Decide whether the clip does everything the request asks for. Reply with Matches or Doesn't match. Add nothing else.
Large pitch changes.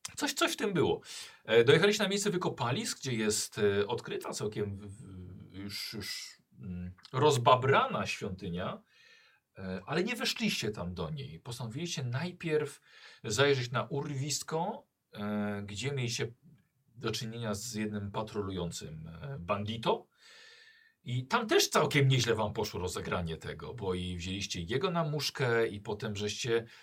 Matches